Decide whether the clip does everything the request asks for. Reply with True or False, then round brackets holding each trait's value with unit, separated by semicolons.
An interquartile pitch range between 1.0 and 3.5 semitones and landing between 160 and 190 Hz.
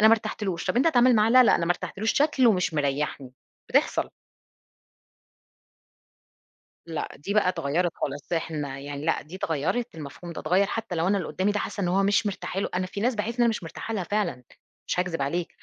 False (4.9 semitones; 185 Hz)